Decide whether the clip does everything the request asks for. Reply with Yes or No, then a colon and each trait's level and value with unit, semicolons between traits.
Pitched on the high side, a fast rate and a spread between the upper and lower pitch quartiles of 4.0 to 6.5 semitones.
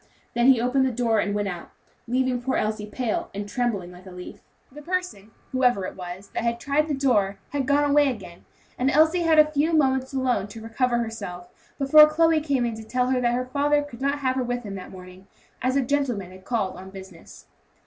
Yes: high, 245 Hz; fast, 220 wpm; wide, 5.4 semitones